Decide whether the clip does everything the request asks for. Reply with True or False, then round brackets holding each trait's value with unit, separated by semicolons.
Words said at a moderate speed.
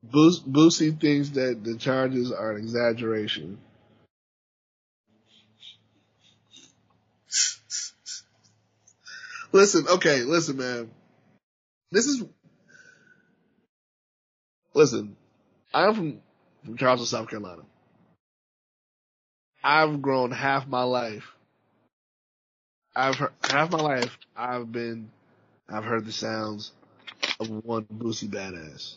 False (85 wpm)